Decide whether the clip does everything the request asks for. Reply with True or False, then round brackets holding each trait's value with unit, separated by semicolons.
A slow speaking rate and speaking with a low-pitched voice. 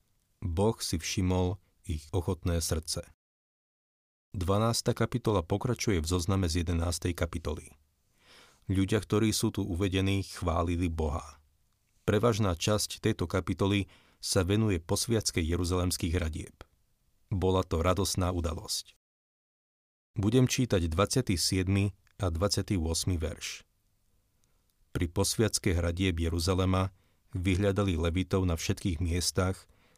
True (100 wpm; 95 Hz)